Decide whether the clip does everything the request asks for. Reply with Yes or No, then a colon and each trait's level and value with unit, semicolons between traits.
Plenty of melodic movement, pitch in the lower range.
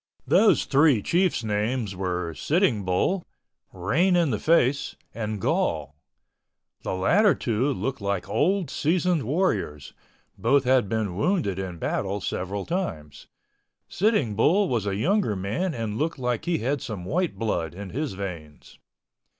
Yes: wide, 9.0 semitones; low, 115 Hz